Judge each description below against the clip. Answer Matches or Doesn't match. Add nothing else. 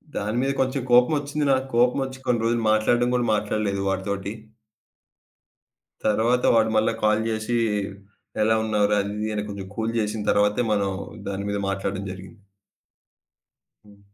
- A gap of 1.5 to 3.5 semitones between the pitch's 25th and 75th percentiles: Matches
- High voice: Doesn't match